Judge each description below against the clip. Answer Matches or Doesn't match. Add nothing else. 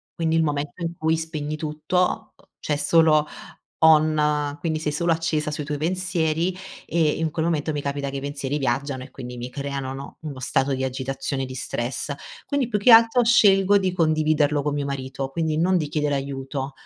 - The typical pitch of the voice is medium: Matches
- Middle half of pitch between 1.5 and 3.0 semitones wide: Matches